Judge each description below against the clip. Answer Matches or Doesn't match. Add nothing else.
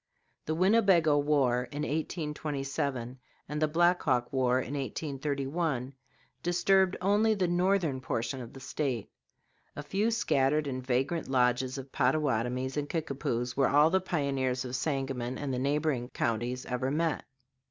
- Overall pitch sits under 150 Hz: Matches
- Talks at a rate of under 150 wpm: Matches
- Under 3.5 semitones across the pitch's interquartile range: Doesn't match